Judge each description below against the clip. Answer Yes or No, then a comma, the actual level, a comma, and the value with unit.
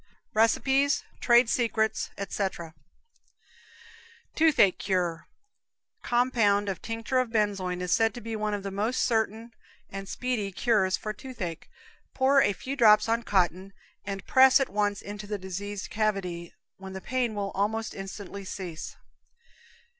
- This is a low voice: No, high, 210 Hz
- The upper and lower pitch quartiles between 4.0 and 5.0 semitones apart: No, average, 3.0 semitones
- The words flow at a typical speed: No, slow, 130 wpm